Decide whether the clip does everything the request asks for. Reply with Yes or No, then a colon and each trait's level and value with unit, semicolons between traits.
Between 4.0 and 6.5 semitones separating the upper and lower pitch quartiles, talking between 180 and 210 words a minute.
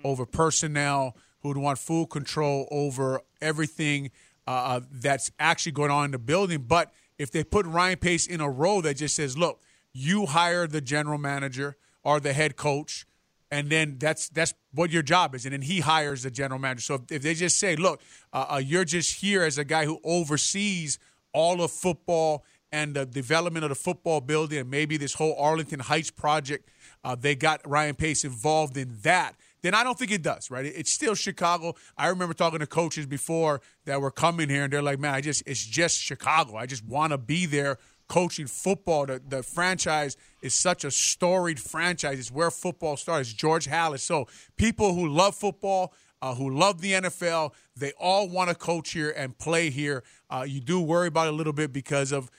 No: average, 3.2 semitones; average, 200 wpm